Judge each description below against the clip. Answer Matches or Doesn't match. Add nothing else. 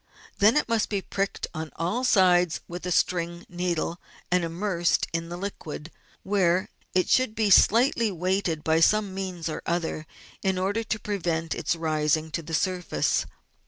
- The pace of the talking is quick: Doesn't match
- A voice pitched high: Doesn't match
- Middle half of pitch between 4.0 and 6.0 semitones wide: Doesn't match